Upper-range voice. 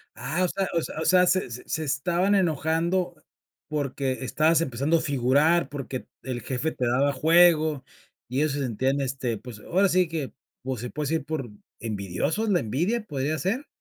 No: medium, 150 Hz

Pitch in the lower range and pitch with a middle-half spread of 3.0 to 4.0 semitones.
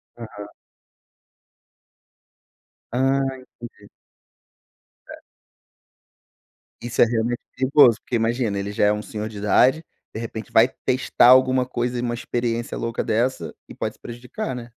No: low, 120 Hz; narrow, 2.4 semitones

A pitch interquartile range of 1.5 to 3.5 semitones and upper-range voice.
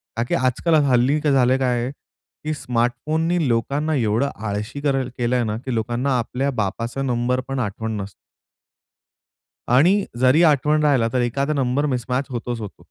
No: average, 3.0 semitones; low, 125 Hz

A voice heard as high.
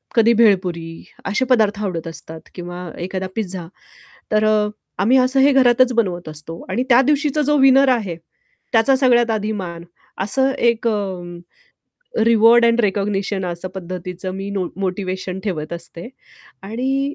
Yes: high, 210 Hz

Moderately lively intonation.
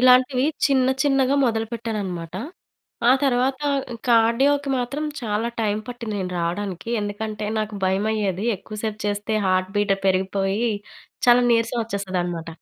Yes: average, 3.7 semitones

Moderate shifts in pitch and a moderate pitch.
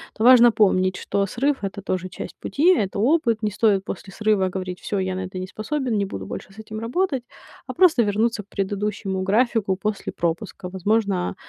No: average, 3.4 semitones; high, 205 Hz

